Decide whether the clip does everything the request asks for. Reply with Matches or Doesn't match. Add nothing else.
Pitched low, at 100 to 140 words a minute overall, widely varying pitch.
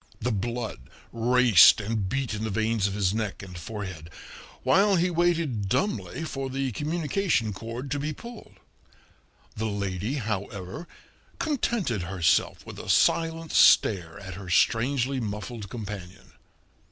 Matches